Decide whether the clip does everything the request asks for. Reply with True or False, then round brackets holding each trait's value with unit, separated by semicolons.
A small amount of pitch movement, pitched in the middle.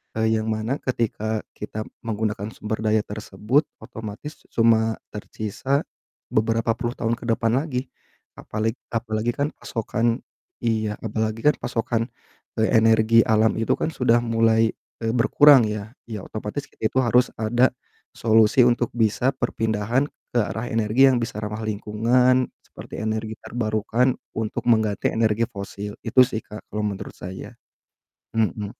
False (1.7 semitones; 110 Hz)